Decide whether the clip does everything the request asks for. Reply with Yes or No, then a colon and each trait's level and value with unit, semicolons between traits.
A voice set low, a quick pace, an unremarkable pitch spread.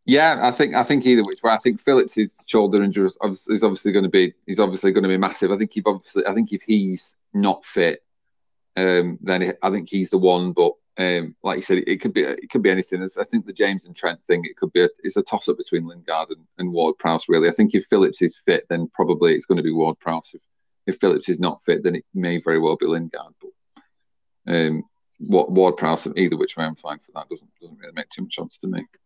Yes: very low, 95 Hz; fast, 245 wpm; average, 3.9 semitones